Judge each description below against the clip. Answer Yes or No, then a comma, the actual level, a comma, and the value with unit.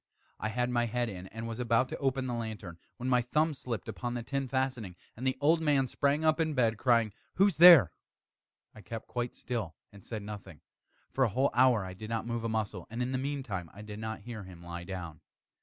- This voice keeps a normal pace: No, fast, 230 wpm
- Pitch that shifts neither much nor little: Yes, average, 3.8 semitones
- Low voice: Yes, low, 115 Hz